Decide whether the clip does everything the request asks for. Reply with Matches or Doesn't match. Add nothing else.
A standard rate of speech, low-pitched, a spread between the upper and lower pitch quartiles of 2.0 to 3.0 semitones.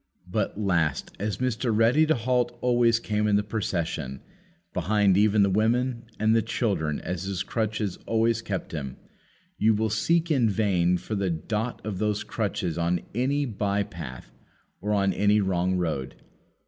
Doesn't match